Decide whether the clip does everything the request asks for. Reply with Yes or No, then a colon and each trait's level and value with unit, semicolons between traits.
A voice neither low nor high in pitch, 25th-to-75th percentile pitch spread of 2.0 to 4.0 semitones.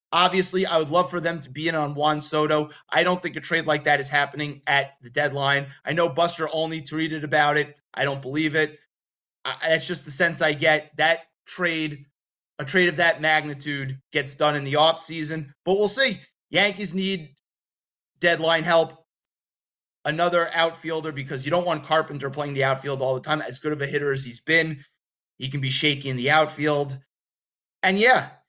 Yes: medium, 155 Hz; narrow, 2.6 semitones